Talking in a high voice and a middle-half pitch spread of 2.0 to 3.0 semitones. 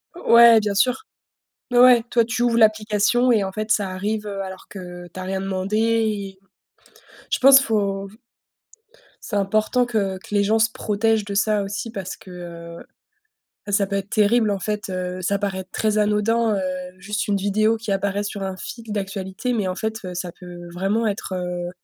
Yes: high, 205 Hz; narrow, 2.5 semitones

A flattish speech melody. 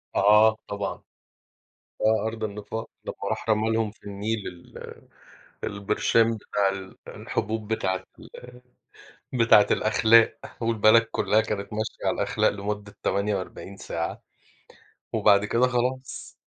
Yes: narrow, 1.8 semitones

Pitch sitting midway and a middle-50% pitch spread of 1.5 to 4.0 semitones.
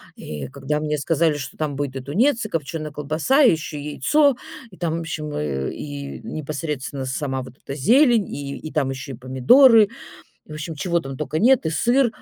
No: medium, 150 Hz; average, 4.6 semitones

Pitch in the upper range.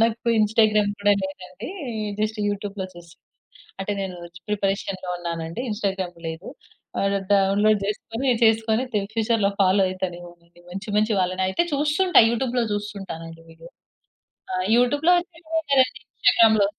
Yes: high, 205 Hz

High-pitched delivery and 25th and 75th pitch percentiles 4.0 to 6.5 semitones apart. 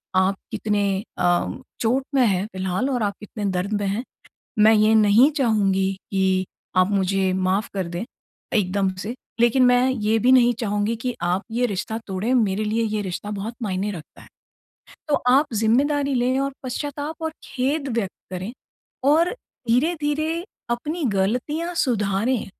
Yes: high, 220 Hz; average, 4.9 semitones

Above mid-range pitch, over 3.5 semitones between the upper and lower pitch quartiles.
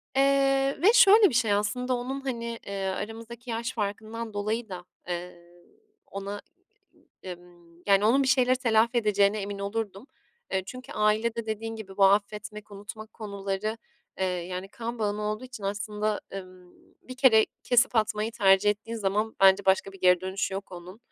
No: high, 210 Hz; average, 3.0 semitones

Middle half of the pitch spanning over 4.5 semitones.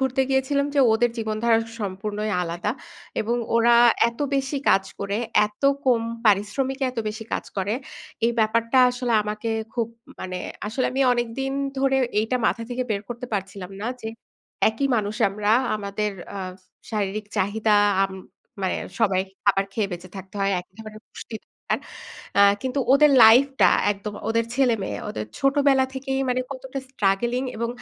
No: average, 4.1 semitones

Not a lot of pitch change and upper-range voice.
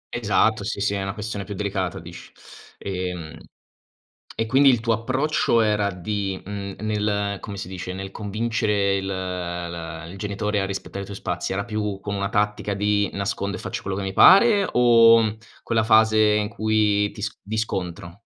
No: narrow, 2.0 semitones; low, 100 Hz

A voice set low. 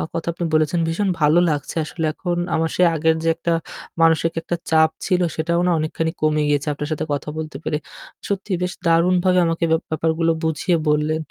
No: medium, 160 Hz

